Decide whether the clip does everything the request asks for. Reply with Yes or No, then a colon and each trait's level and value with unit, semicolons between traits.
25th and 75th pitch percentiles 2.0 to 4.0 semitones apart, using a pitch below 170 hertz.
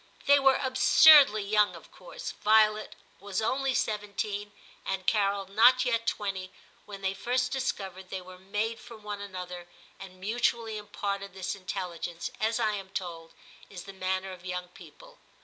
No: average, 2.9 semitones; high, 200 Hz